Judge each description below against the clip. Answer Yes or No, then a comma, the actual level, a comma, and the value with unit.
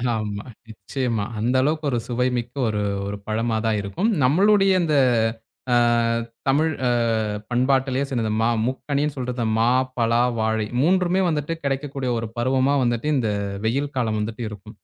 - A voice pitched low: Yes, low, 125 Hz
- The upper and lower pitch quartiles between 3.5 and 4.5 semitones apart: Yes, average, 4.2 semitones